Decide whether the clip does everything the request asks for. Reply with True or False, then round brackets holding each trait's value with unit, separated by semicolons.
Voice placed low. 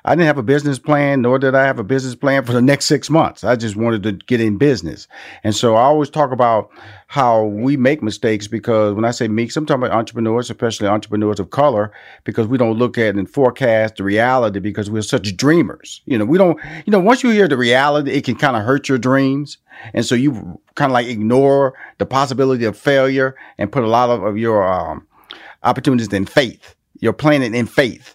True (125 Hz)